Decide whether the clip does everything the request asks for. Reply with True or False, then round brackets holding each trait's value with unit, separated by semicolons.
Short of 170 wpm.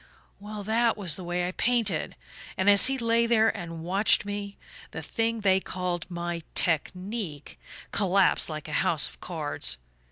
True (160 wpm)